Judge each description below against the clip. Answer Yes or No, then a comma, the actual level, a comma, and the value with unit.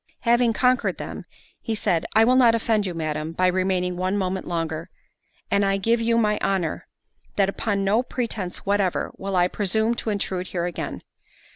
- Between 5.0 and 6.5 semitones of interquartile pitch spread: No, average, 3.7 semitones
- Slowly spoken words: No, average, 175 wpm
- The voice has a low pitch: No, high, 195 Hz